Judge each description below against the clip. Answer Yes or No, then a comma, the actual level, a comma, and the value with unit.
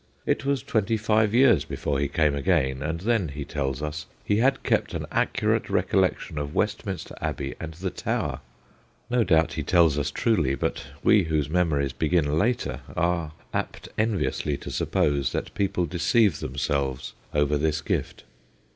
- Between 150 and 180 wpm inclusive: Yes, average, 165 wpm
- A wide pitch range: Yes, wide, 6.1 semitones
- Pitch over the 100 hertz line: No, very low, 80 Hz